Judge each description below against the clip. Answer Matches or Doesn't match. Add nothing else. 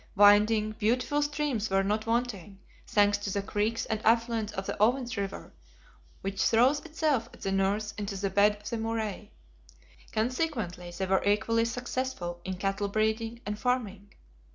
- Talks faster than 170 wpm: Doesn't match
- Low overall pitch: Doesn't match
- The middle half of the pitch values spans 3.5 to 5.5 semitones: Doesn't match